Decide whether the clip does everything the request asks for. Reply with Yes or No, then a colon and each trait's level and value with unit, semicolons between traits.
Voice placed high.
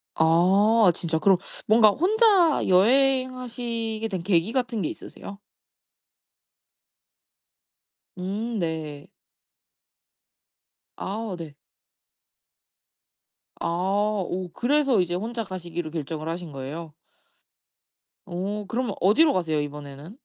Yes: high, 195 Hz